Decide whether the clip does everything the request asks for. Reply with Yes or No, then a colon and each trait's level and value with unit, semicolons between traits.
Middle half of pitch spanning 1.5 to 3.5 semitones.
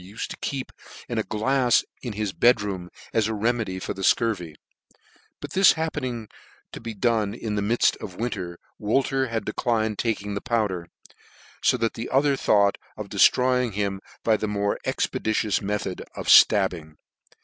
Yes: average, 3.0 semitones